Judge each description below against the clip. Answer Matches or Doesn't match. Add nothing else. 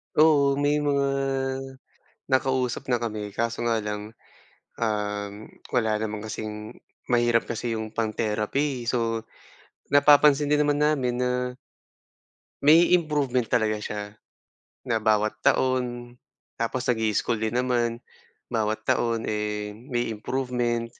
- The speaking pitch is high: Doesn't match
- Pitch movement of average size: Matches